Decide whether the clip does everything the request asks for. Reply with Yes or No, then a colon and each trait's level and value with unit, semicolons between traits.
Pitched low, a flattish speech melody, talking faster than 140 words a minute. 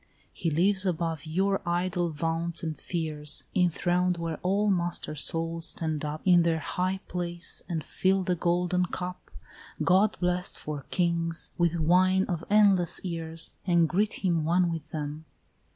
No: medium, 175 Hz; narrow, 1.9 semitones; average, 150 wpm